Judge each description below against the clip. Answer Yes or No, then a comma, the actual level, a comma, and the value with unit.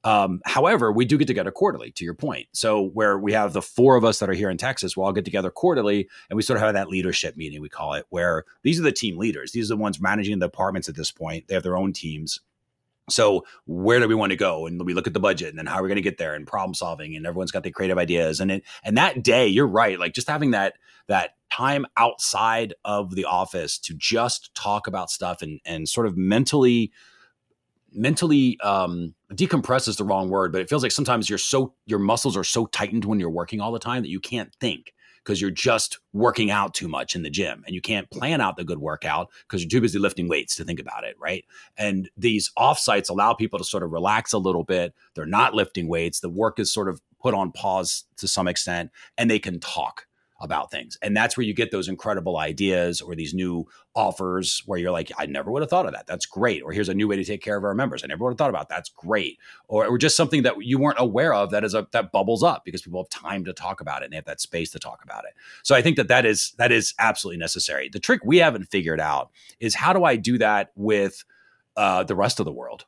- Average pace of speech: No, fast, 255 wpm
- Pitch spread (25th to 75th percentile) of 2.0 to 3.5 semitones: No, average, 3.9 semitones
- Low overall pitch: Yes, low, 100 Hz